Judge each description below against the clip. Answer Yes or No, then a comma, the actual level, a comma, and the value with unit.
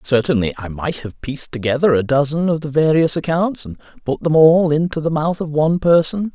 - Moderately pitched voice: Yes, medium, 150 Hz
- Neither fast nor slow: No, fast, 210 wpm